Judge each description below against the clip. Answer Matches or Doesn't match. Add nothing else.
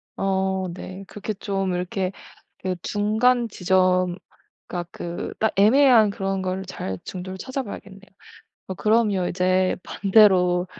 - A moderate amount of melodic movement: Doesn't match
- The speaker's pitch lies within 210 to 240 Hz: Doesn't match